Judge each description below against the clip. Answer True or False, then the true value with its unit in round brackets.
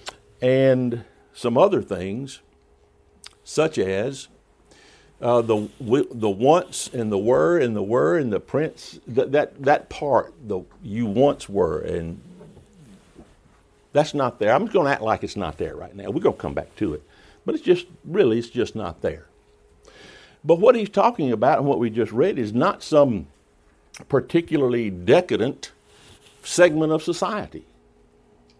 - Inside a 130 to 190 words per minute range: True (155 wpm)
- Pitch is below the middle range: True (120 Hz)